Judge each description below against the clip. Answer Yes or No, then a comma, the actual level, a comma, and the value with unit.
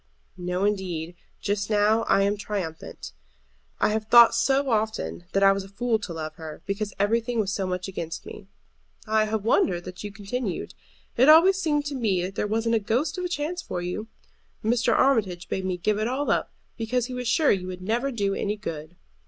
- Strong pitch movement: No, average, 4.2 semitones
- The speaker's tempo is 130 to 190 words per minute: No, fast, 205 wpm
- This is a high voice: Yes, high, 210 Hz